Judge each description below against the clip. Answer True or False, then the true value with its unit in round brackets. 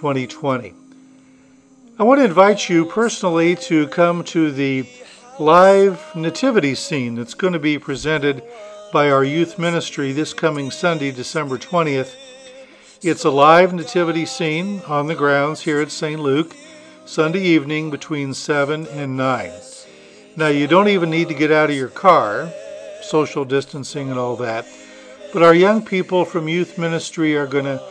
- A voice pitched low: False (160 Hz)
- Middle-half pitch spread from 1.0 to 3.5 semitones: False (4.6 semitones)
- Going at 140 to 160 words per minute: True (155 wpm)